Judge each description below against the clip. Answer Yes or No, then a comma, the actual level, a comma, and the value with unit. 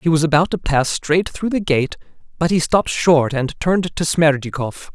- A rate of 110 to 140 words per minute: No, fast, 205 wpm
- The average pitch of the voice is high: No, medium, 155 Hz